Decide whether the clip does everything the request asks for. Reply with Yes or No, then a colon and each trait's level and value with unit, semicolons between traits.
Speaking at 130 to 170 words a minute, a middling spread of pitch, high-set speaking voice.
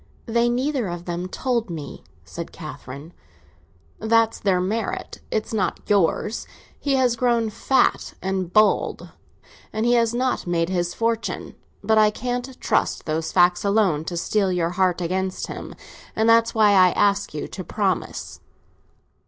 Yes: average, 150 wpm; average, 4.3 semitones; high, 205 Hz